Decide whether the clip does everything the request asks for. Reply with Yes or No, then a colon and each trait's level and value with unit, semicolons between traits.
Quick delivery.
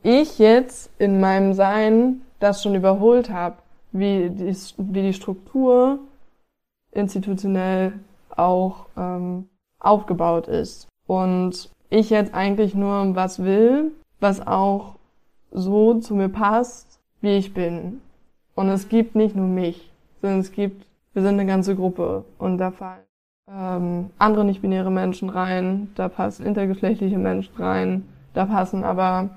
No: average, 130 wpm